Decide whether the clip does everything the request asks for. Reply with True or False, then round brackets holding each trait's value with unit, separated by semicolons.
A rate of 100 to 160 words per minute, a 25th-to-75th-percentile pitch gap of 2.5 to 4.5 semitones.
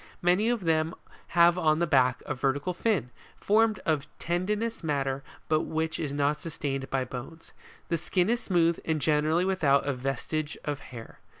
False (170 wpm; 3.9 semitones)